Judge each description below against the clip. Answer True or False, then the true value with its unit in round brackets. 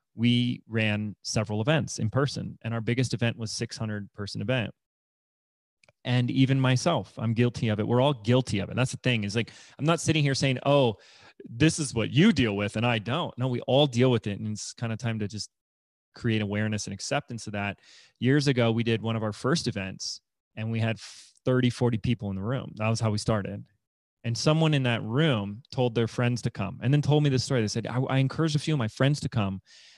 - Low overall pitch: True (120 Hz)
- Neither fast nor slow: False (230 wpm)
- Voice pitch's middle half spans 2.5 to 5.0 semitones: True (3.4 semitones)